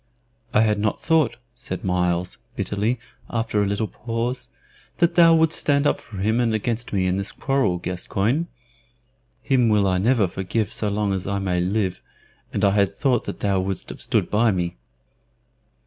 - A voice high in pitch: No, low, 105 Hz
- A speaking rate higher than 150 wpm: Yes, average, 180 wpm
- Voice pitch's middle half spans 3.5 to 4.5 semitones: Yes, average, 3.8 semitones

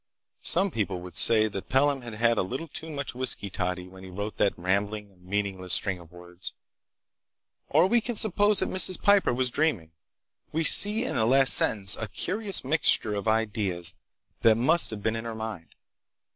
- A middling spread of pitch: No, wide, 7.7 semitones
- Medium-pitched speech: No, low, 110 Hz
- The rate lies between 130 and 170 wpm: No, average, 185 wpm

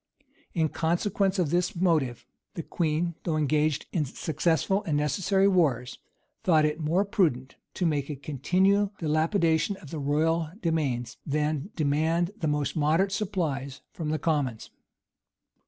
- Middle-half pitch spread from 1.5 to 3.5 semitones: Yes, average, 3.2 semitones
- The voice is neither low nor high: Yes, medium, 160 Hz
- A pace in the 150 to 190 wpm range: No, average, 140 wpm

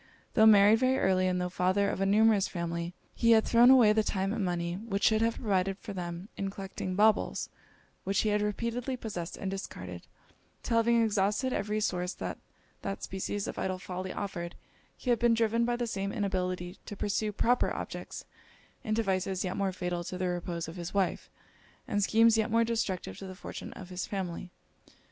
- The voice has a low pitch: No, high, 195 Hz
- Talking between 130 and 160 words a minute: No, average, 195 wpm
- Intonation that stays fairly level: No, average, 3.2 semitones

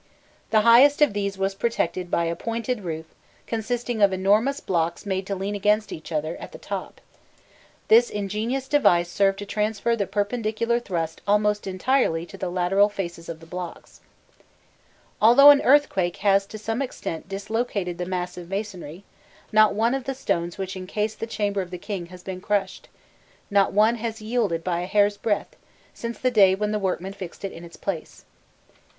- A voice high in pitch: Yes, high, 200 Hz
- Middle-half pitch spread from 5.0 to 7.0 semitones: No, average, 3.5 semitones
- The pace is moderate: Yes, average, 180 wpm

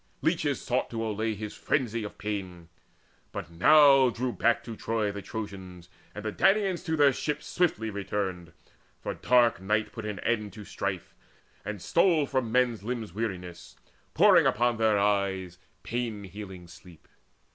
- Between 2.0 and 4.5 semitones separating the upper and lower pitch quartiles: Yes, average, 3.7 semitones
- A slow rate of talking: No, average, 155 wpm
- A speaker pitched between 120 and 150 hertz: No, low, 105 Hz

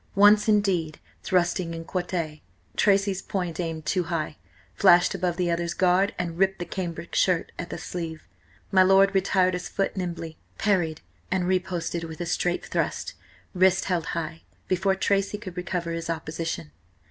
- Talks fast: No, average, 160 wpm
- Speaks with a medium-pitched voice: Yes, medium, 180 Hz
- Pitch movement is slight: Yes, narrow, 2.3 semitones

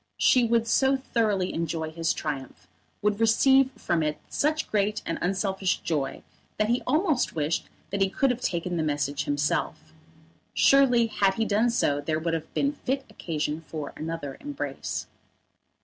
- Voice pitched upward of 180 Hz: Yes, high, 190 Hz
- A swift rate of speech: No, average, 160 wpm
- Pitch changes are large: Yes, wide, 7.2 semitones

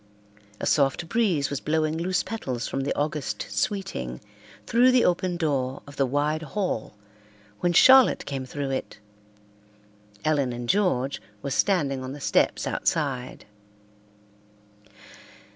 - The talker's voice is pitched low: No, medium, 145 Hz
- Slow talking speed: Yes, slow, 125 wpm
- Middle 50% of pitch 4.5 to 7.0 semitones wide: Yes, average, 4.8 semitones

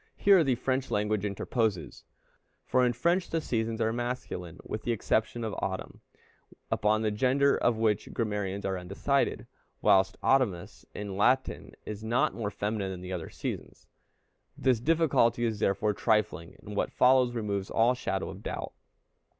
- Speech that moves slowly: No, average, 155 wpm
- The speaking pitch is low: Yes, low, 110 Hz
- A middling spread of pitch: Yes, average, 3.8 semitones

